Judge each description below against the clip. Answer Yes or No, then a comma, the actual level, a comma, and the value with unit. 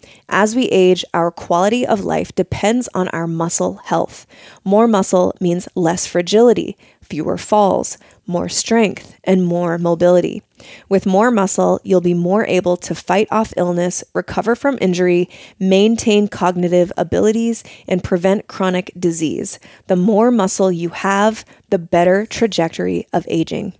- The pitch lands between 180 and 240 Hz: Yes, medium, 185 Hz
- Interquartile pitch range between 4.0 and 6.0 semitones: No, average, 3.0 semitones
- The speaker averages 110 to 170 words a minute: Yes, average, 140 wpm